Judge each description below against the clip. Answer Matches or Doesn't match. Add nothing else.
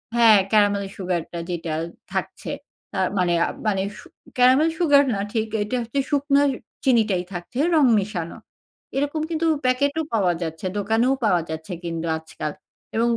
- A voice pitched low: Doesn't match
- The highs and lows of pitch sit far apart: Matches